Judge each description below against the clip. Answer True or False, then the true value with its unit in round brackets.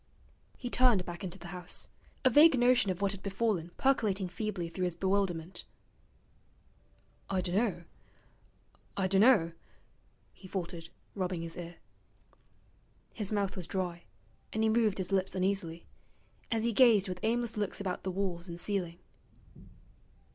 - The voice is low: False (190 Hz)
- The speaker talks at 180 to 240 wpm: False (140 wpm)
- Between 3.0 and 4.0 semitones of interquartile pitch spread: True (3.4 semitones)